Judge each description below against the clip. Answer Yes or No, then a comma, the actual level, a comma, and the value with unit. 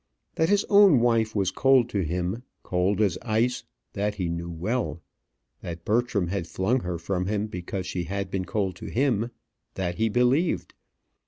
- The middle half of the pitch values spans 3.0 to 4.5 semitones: No, average, 5.0 semitones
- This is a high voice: No, low, 100 Hz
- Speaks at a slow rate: No, average, 170 wpm